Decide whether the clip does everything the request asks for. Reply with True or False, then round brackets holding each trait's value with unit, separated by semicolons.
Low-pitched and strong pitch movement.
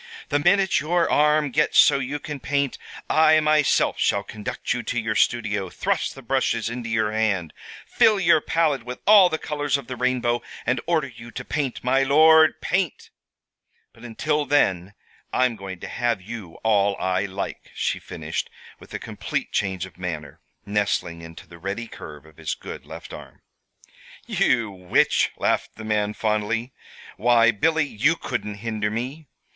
True (120 Hz; 6.0 semitones)